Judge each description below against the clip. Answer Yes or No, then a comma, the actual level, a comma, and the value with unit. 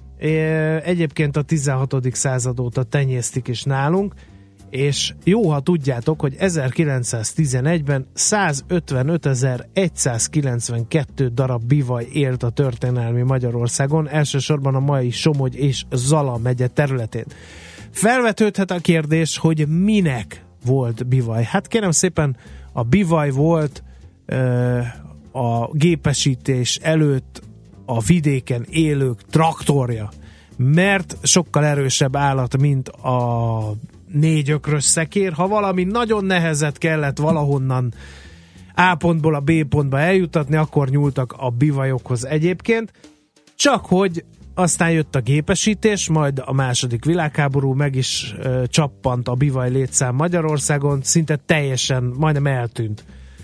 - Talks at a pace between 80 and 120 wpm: Yes, average, 110 wpm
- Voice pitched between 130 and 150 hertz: Yes, medium, 140 Hz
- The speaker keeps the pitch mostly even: No, average, 4.2 semitones